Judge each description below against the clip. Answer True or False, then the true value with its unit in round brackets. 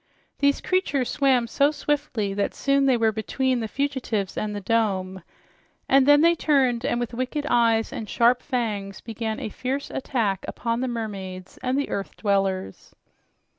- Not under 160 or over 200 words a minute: True (165 wpm)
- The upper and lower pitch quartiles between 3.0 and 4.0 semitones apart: False (4.6 semitones)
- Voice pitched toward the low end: False (235 Hz)